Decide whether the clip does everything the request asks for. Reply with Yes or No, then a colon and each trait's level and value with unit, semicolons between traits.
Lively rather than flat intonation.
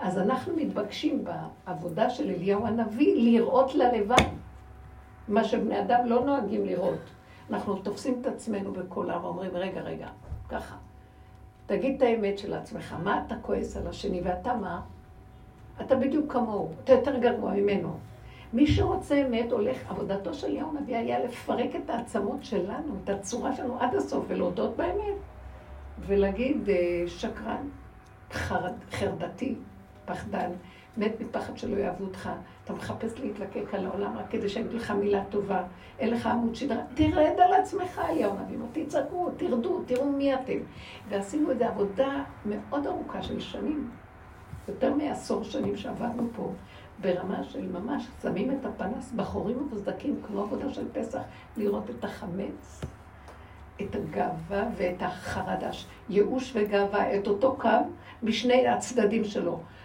No: average, 4.8 semitones